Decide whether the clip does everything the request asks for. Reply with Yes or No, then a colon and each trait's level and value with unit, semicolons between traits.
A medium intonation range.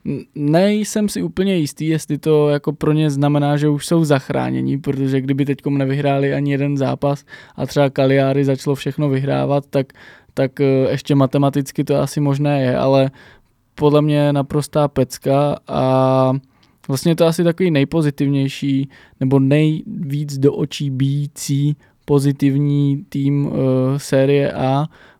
No: narrow, 1.4 semitones